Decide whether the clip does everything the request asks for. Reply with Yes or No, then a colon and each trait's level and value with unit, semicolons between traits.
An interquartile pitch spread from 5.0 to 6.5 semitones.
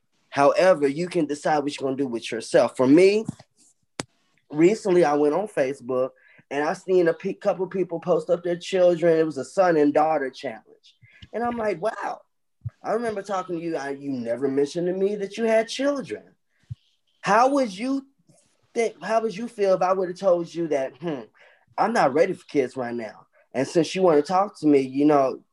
Yes: wide, 5.6 semitones